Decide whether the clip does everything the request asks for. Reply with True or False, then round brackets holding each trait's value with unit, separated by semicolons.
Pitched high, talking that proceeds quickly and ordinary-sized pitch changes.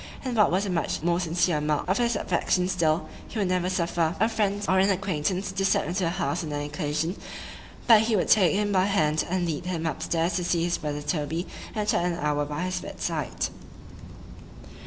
False (180 Hz; 220 wpm; 3.4 semitones)